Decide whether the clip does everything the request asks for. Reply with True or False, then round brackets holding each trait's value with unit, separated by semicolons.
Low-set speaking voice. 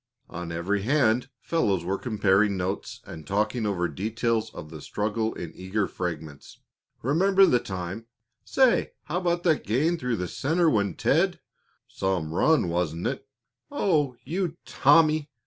True (110 Hz)